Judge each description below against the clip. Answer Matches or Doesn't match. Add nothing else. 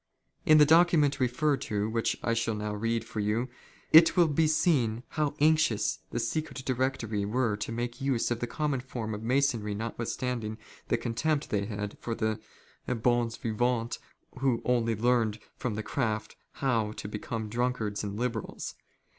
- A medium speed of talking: Matches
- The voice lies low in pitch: Matches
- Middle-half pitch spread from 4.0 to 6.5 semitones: Doesn't match